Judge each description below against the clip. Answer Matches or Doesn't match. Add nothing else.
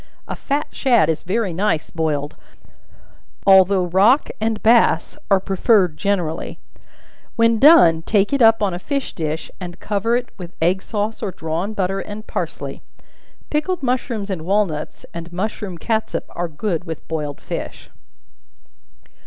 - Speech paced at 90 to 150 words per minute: Matches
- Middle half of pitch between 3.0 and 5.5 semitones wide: Matches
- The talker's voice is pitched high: Matches